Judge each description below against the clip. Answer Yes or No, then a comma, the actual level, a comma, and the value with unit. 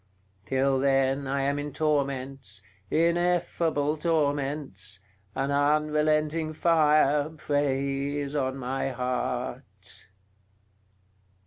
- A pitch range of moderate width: No, narrow, 2.3 semitones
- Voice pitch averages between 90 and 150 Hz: Yes, medium, 140 Hz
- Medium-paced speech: No, slow, 80 wpm